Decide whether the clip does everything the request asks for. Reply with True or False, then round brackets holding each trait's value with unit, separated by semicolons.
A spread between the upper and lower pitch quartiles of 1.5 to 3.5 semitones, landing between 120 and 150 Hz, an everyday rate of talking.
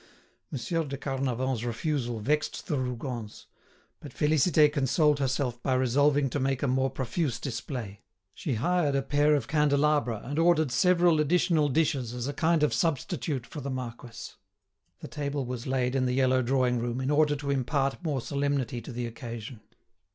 True (3.1 semitones; 135 Hz; 165 wpm)